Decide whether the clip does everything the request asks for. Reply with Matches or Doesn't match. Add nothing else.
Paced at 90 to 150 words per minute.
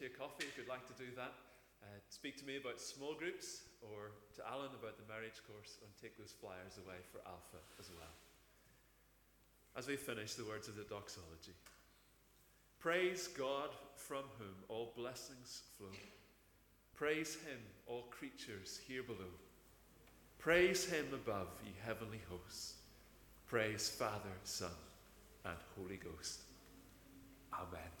Matches